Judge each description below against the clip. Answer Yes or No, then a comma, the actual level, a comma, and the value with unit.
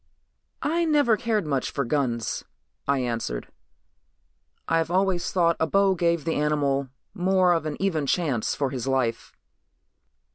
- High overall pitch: No, medium, 160 Hz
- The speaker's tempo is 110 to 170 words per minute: Yes, average, 140 wpm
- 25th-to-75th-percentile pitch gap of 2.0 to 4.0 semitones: No, wide, 5.5 semitones